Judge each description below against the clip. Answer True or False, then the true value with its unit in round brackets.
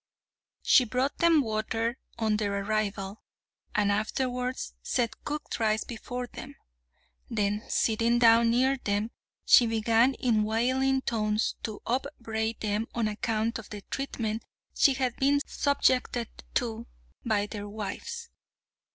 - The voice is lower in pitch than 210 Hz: False (230 Hz)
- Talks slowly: True (125 wpm)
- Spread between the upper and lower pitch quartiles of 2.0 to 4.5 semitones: True (2.7 semitones)